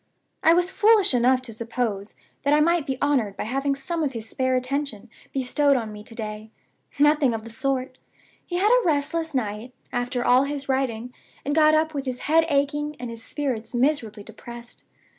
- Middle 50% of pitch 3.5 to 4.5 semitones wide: Yes, average, 3.9 semitones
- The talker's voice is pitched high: Yes, very high, 265 Hz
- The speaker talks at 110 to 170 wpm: No, average, 190 wpm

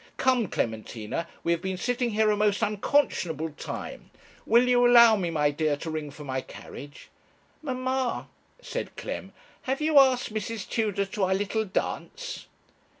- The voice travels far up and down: Yes, wide, 7.3 semitones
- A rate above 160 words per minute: No, average, 155 wpm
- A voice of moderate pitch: No, high, 210 Hz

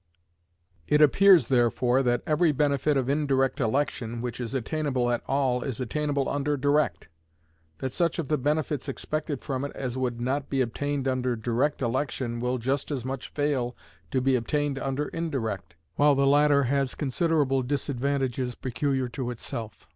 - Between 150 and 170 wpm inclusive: Yes, average, 160 wpm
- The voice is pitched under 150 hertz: Yes, low, 135 Hz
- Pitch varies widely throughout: No, average, 2.8 semitones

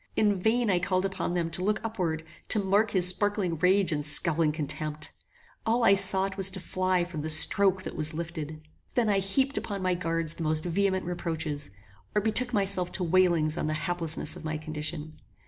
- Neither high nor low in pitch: Yes, medium, 180 Hz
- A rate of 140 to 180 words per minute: No, average, 195 wpm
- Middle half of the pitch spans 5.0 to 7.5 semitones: No, average, 3.7 semitones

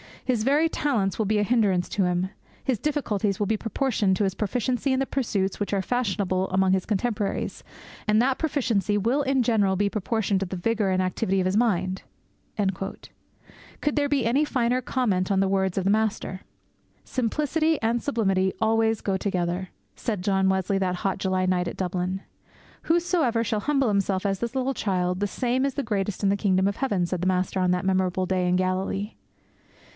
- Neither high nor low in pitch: No, high, 200 Hz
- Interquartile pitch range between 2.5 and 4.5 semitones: Yes, average, 4.1 semitones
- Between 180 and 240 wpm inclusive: Yes, average, 190 wpm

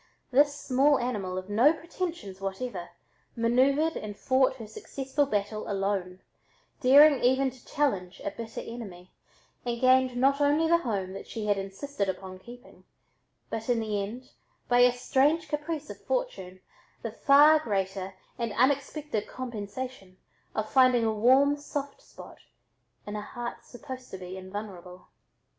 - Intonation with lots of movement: Yes, wide, 5.7 semitones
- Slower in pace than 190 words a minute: Yes, average, 145 wpm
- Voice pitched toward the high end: Yes, high, 245 Hz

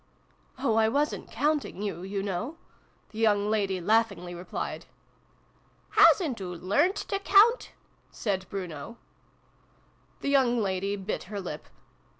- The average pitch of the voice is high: Yes, high, 205 Hz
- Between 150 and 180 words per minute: No, average, 140 wpm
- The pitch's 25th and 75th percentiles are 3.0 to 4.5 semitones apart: No, wide, 5.5 semitones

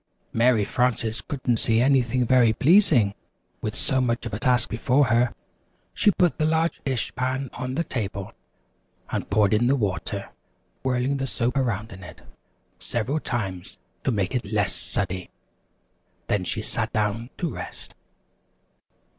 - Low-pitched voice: Yes, low, 120 Hz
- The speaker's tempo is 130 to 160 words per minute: Yes, average, 155 wpm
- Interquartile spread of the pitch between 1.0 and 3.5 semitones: No, average, 3.9 semitones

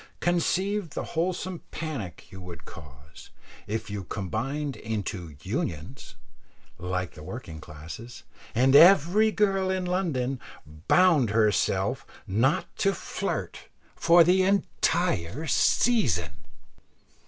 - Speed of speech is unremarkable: No, slow, 105 wpm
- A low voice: Yes, low, 130 Hz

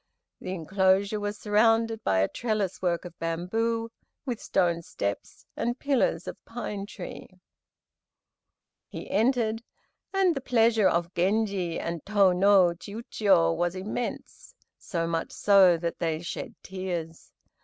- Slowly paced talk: Yes, slow, 130 wpm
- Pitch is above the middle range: Yes, high, 195 Hz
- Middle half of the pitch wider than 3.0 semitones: Yes, average, 4.6 semitones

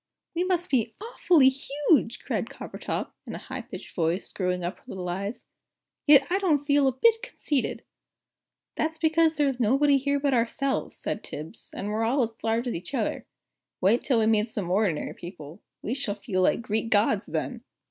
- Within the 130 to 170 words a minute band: No, average, 190 wpm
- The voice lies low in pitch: No, high, 240 Hz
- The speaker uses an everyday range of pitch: No, wide, 5.9 semitones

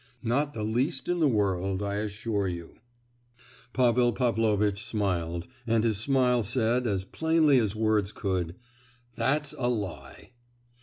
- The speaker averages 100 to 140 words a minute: Yes, slow, 135 wpm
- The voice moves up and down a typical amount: Yes, average, 3.9 semitones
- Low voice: Yes, low, 110 Hz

